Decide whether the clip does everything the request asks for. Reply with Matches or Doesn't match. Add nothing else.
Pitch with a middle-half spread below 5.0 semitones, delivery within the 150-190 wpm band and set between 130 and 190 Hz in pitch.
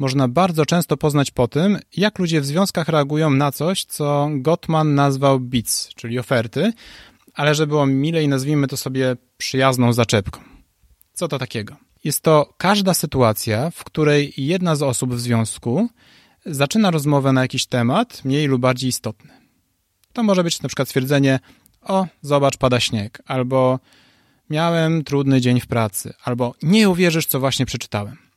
Matches